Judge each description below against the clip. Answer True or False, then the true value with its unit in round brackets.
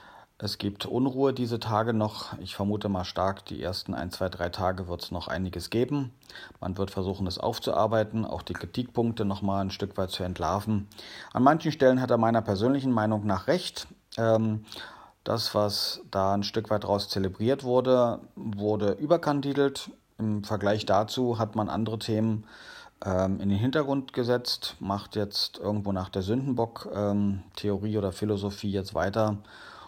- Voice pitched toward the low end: True (105 Hz)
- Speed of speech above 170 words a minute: False (165 wpm)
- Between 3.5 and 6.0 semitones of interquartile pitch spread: False (2.8 semitones)